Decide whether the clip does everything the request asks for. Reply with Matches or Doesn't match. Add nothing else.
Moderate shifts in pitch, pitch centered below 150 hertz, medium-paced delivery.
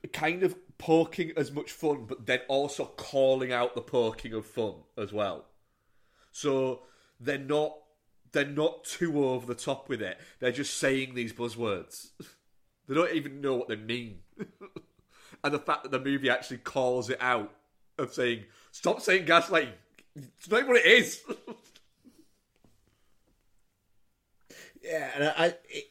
Matches